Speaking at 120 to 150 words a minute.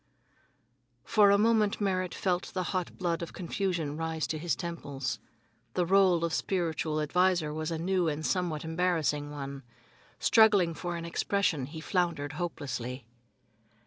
Yes: average, 140 wpm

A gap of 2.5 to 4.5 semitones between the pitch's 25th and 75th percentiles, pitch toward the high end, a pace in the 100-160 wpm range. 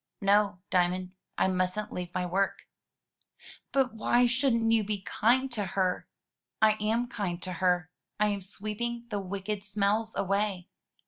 Yes: average, 3.3 semitones; high, 205 Hz; average, 145 wpm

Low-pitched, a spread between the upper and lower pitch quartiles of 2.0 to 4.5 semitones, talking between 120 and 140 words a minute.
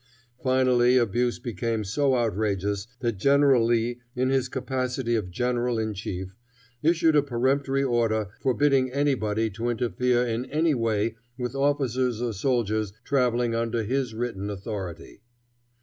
Yes: low, 120 Hz; average, 3.0 semitones; slow, 135 wpm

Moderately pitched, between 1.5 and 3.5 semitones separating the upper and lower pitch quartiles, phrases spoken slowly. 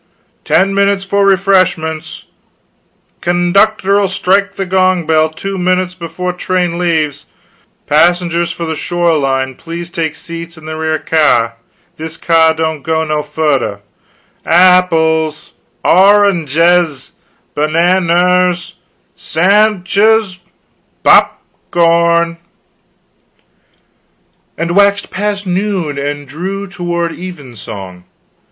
Yes: medium, 170 Hz; average, 2.8 semitones; slow, 110 wpm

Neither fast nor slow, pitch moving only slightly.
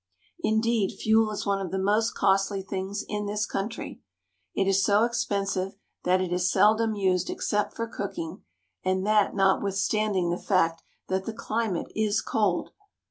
Yes: average, 155 wpm; narrow, 2.1 semitones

